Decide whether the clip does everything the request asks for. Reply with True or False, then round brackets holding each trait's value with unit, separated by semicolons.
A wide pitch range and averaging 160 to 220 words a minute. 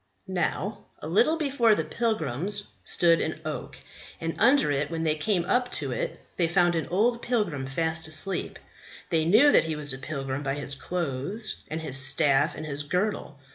True (6.3 semitones; 180 wpm)